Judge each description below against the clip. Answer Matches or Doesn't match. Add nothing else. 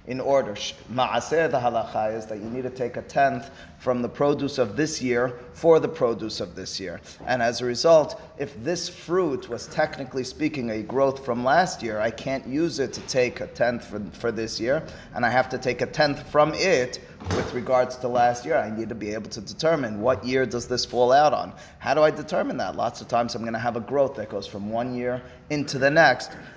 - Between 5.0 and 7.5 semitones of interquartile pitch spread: Doesn't match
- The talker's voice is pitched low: Matches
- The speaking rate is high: Matches